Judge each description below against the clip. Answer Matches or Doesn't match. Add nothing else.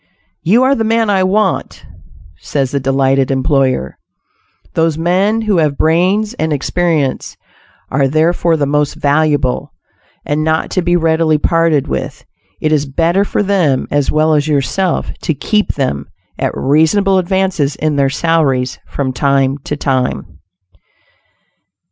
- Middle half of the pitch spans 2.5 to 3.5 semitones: Doesn't match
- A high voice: Doesn't match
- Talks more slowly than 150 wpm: Matches